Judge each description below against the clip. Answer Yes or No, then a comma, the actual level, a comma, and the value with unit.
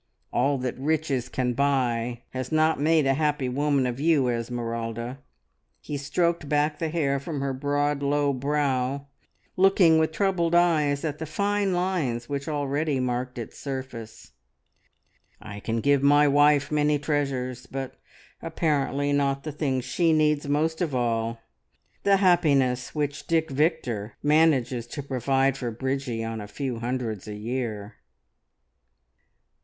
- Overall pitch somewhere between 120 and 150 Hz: Yes, medium, 140 Hz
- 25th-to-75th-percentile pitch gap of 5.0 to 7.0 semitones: No, average, 3.3 semitones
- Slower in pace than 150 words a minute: Yes, average, 140 wpm